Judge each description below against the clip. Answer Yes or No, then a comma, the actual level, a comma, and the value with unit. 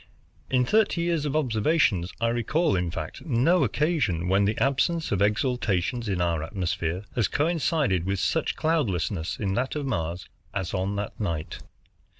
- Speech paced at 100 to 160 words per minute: Yes, average, 155 wpm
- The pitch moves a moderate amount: No, wide, 8.1 semitones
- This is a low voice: Yes, low, 110 Hz